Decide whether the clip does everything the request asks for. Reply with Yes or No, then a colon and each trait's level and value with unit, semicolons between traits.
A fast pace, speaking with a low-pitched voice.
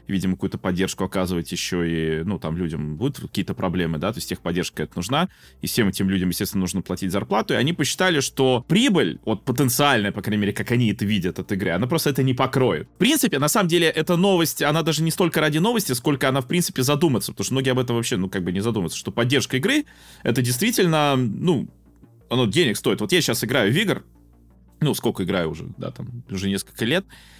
Yes: fast, 220 wpm; low, 120 Hz